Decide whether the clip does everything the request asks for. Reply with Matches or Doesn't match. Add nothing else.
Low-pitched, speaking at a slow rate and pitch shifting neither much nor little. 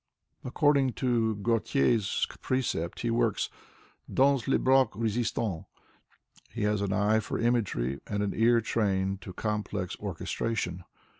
Matches